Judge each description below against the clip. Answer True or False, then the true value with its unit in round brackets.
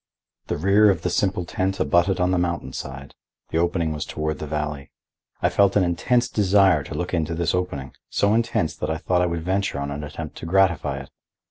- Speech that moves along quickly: True (210 wpm)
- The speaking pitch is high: False (85 Hz)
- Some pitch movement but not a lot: True (3.8 semitones)